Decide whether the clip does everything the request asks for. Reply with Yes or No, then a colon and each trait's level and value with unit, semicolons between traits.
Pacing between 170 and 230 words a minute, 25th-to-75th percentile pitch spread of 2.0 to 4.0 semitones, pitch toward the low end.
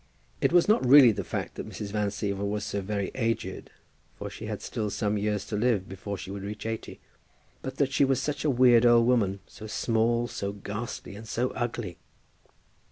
Yes: average, 200 wpm; average, 3.1 semitones; low, 110 Hz